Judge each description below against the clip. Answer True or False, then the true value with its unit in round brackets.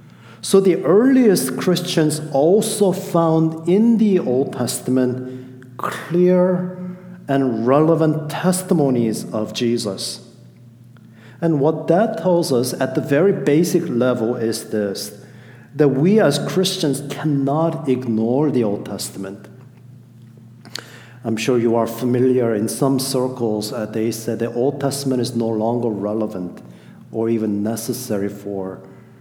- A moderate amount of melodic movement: False (5.7 semitones)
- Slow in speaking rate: True (120 wpm)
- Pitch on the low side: True (130 Hz)